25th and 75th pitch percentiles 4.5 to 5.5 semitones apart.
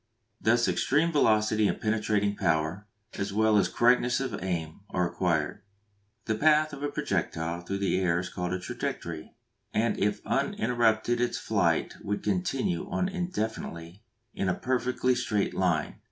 Yes: average, 5.1 semitones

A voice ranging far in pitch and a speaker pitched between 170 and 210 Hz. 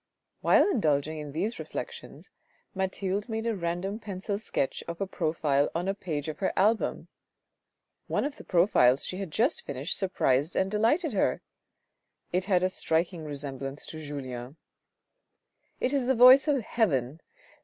Yes: wide, 6.3 semitones; medium, 185 Hz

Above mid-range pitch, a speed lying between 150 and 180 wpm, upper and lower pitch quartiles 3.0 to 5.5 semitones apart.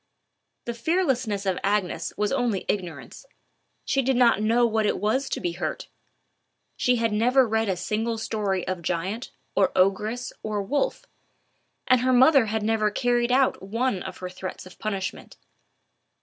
Yes: high, 220 Hz; average, 160 wpm; average, 4.0 semitones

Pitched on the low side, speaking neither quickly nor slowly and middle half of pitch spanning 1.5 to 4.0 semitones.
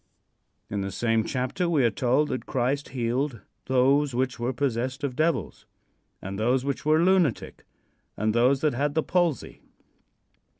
Yes: low, 130 Hz; average, 155 wpm; average, 3.5 semitones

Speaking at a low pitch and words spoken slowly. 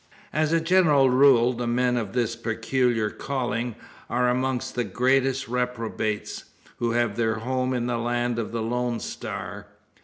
No: low, 120 Hz; average, 155 wpm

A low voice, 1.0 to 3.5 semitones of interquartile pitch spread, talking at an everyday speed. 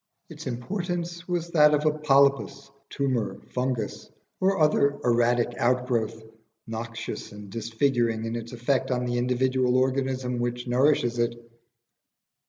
No: low, 125 Hz; average, 3.0 semitones; slow, 125 wpm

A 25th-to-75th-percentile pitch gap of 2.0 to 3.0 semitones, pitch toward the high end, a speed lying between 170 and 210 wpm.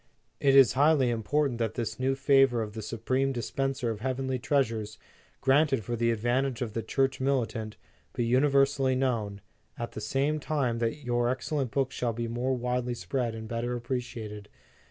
No: average, 2.7 semitones; low, 125 Hz; average, 175 wpm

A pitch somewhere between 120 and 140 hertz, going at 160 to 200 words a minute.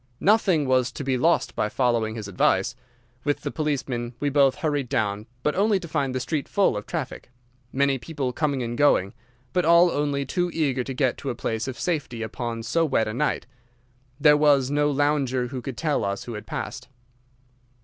Yes: low, 135 Hz; average, 195 wpm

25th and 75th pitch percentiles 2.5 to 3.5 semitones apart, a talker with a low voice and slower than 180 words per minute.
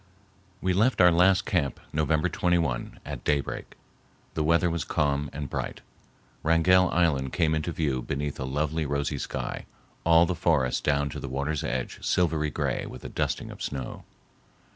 Yes: average, 3.1 semitones; very low, 75 Hz; average, 165 wpm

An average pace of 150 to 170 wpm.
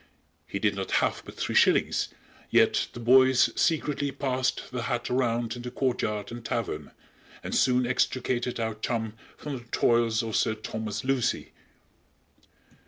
Yes: average, 155 wpm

